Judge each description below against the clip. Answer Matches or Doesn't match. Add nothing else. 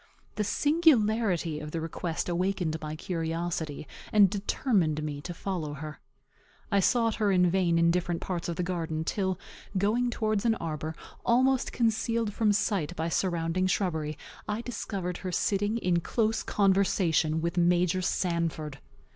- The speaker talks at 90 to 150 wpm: Matches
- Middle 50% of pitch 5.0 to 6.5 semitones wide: Doesn't match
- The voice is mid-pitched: Matches